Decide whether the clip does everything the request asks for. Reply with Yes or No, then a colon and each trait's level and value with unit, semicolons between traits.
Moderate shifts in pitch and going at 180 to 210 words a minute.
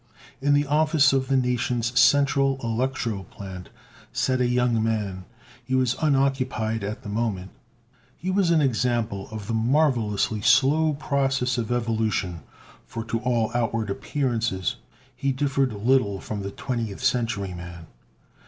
No: average, 3.8 semitones; average, 140 wpm